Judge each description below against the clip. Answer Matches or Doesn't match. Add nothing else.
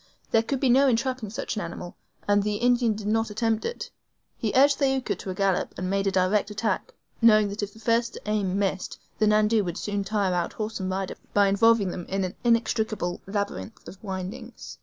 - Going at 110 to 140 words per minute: Doesn't match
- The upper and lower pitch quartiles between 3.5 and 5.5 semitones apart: Doesn't match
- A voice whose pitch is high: Matches